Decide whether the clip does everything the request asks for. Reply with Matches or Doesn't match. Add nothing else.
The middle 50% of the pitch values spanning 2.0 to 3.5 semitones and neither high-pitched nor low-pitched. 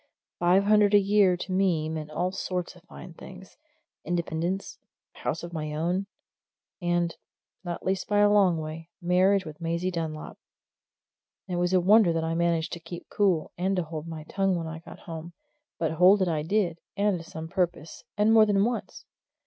Matches